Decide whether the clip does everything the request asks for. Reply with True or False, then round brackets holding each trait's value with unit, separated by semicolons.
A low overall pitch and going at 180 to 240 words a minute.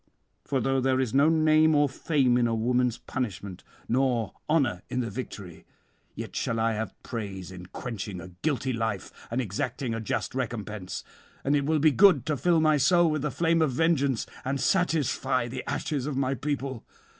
True (130 Hz; 185 wpm)